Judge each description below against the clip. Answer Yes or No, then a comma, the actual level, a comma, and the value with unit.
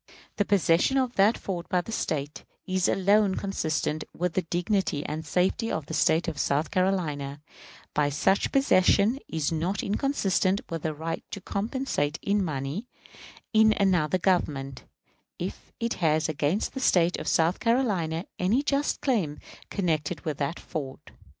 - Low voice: No, medium, 180 Hz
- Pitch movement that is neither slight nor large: Yes, average, 4.6 semitones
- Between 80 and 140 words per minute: No, average, 150 wpm